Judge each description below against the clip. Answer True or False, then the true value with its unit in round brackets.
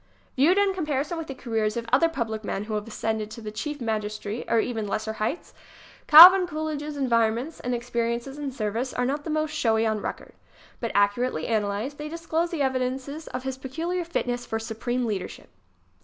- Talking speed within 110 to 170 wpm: False (195 wpm)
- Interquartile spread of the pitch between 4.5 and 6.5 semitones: True (5.2 semitones)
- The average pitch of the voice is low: False (250 Hz)